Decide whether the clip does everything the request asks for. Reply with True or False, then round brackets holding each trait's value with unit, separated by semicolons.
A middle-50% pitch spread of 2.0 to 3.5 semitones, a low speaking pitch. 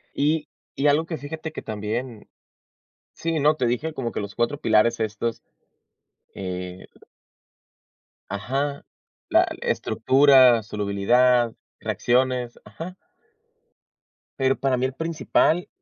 False (4.7 semitones; 125 Hz)